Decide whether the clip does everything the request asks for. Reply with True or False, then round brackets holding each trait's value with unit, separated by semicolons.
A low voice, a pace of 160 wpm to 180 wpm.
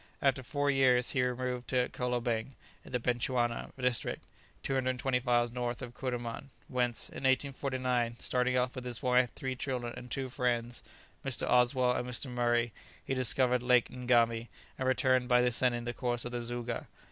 True (125 Hz; 165 wpm)